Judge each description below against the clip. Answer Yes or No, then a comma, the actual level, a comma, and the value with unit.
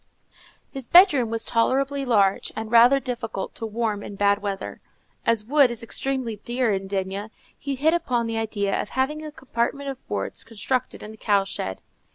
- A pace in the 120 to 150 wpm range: No, average, 180 wpm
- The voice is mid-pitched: No, high, 230 Hz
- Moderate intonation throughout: Yes, average, 4.3 semitones